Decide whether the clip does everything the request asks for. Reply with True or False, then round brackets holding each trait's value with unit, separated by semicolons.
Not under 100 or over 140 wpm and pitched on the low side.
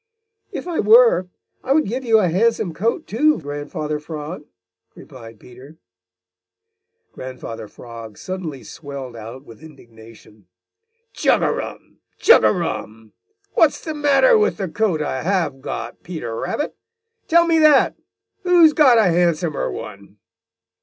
False (135 wpm; 165 Hz)